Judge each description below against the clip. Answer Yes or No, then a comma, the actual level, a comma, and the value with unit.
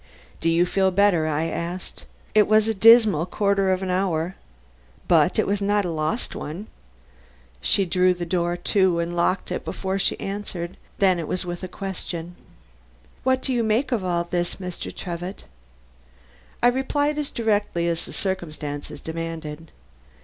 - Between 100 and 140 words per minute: No, average, 165 wpm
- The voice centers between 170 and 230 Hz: Yes, medium, 185 Hz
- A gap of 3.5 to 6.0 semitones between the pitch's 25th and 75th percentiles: No, average, 3.1 semitones